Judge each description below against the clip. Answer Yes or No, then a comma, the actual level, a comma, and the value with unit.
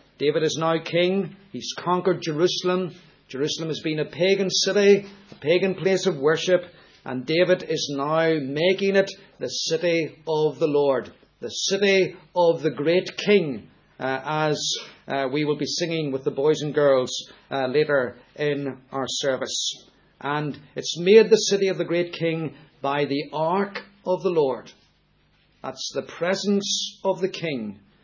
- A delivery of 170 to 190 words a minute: No, average, 155 wpm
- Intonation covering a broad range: No, average, 4.2 semitones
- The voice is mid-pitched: Yes, medium, 165 Hz